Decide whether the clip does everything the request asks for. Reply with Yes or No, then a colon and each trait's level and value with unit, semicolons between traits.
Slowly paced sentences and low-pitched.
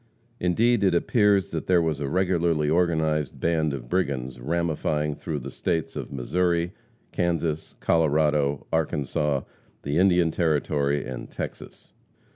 Yes: slow, 125 wpm; very low, 80 Hz